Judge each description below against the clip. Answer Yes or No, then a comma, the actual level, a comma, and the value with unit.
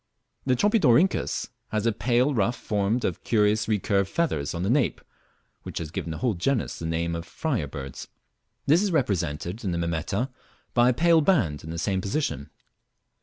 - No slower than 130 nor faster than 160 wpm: No, average, 175 wpm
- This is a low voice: Yes, low, 105 Hz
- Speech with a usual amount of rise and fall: No, wide, 7.4 semitones